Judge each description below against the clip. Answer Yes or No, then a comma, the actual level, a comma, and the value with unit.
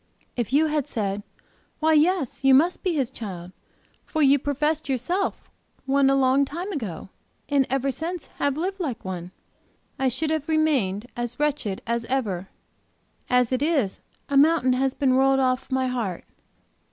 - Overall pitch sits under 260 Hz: No, very high, 270 Hz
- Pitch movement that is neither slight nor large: Yes, average, 3.9 semitones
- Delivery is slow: No, average, 165 wpm